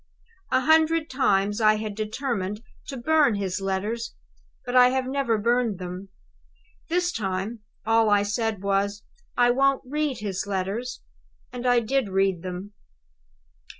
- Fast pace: No, average, 140 wpm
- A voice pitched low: No, high, 220 Hz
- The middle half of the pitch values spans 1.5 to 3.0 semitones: No, average, 4.4 semitones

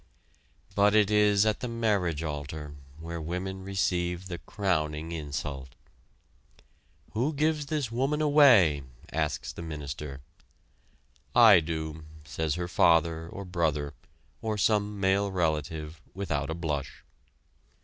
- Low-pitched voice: Yes, very low, 85 Hz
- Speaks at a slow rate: Yes, slow, 120 wpm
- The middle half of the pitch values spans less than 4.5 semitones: No, average, 5.1 semitones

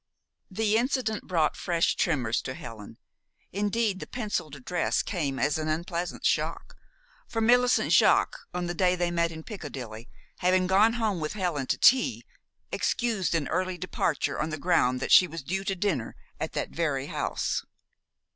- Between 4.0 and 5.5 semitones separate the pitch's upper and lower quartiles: Yes, average, 5.0 semitones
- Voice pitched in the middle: Yes, medium, 175 Hz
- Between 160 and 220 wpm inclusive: Yes, average, 165 wpm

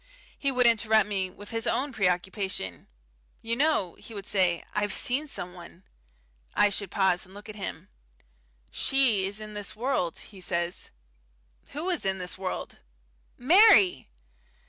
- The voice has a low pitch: No, high, 205 Hz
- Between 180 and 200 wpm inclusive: No, average, 145 wpm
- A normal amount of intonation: Yes, average, 3.9 semitones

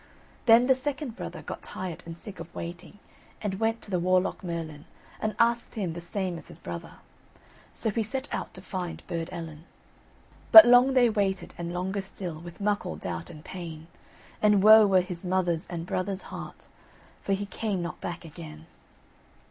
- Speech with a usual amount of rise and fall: Yes, average, 3.8 semitones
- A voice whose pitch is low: No, medium, 185 Hz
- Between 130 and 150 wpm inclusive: No, average, 180 wpm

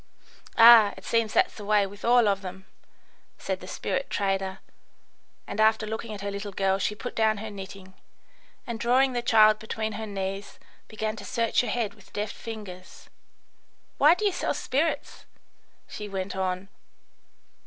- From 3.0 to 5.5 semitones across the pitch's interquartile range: No, narrow, 2.6 semitones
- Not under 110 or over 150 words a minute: No, average, 165 wpm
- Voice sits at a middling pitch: No, high, 215 Hz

